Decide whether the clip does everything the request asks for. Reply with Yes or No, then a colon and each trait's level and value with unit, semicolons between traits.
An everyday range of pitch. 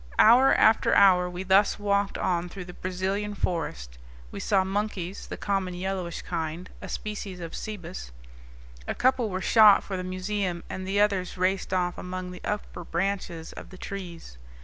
No: narrow, 2.1 semitones